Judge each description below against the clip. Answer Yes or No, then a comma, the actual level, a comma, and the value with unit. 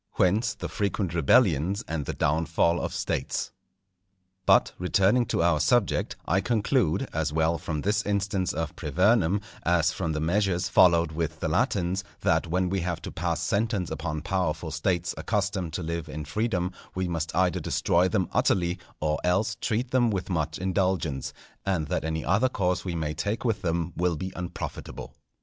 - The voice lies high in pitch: No, very low, 90 Hz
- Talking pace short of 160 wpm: No, average, 170 wpm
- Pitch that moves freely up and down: No, average, 3.5 semitones